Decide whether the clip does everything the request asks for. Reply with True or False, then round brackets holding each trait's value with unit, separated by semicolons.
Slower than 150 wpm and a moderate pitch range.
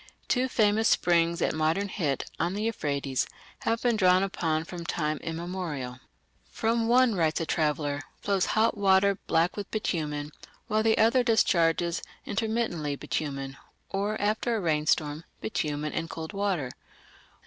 False (140 wpm; 5.7 semitones)